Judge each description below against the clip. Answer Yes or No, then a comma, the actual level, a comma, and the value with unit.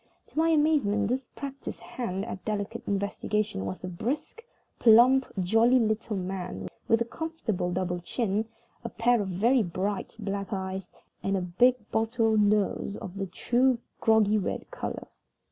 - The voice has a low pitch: No, high, 210 Hz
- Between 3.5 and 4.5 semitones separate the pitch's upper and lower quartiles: Yes, average, 4.0 semitones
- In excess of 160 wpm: No, average, 150 wpm